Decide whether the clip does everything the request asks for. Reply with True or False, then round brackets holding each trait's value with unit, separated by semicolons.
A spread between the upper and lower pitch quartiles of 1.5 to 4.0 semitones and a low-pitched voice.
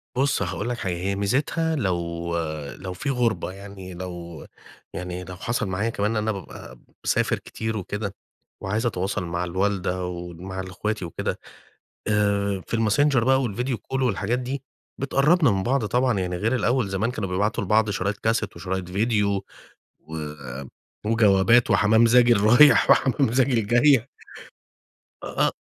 False (4.5 semitones; 105 Hz)